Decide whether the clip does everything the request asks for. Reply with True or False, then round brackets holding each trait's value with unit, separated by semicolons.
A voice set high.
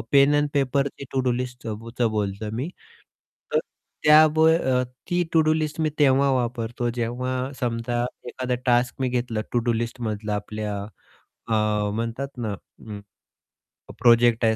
False (120 Hz)